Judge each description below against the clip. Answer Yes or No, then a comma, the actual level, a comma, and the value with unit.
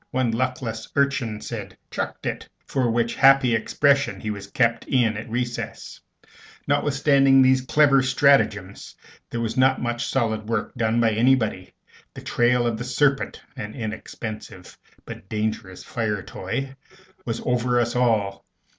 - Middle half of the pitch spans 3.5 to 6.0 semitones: No, average, 3.1 semitones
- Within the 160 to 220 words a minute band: No, average, 140 wpm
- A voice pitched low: Yes, low, 120 Hz